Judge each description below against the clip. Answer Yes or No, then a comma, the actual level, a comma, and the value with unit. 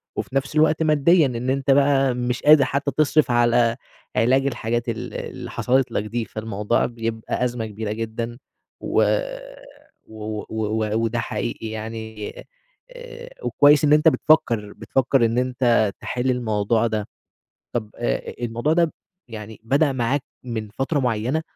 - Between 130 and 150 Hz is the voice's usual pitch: No, low, 120 Hz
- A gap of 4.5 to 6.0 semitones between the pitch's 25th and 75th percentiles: No, average, 3.6 semitones